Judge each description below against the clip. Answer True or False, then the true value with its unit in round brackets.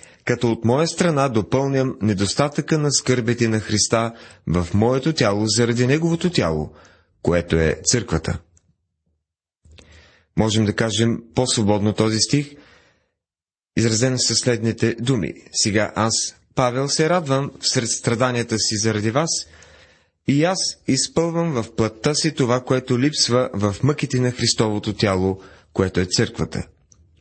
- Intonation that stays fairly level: False (5.5 semitones)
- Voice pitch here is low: True (115 Hz)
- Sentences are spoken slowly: False (125 wpm)